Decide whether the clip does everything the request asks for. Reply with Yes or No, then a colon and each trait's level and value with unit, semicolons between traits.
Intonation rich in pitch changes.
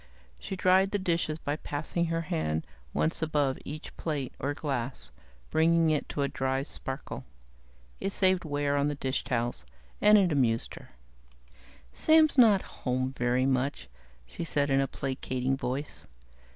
No: average, 4.0 semitones